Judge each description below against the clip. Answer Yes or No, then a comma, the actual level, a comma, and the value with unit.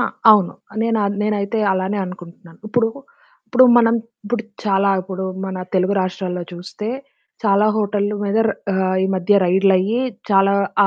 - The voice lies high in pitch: Yes, high, 200 Hz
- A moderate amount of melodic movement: No, narrow, 2.1 semitones